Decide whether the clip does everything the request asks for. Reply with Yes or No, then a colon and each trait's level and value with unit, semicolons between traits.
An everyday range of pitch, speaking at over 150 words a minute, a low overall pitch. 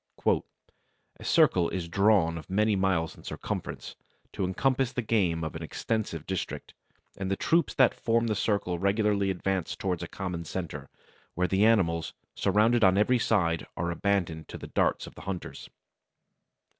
Yes: average, 4.0 semitones; average, 160 wpm; very low, 95 Hz